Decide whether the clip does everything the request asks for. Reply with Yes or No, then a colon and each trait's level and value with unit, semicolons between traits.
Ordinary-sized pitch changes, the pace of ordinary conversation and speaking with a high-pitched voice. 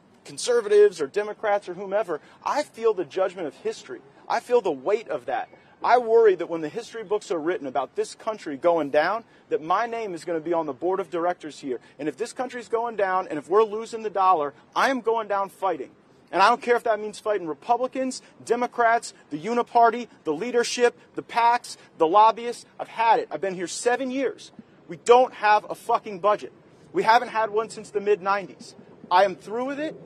No: average, 4.0 semitones; fast, 210 wpm; high, 220 Hz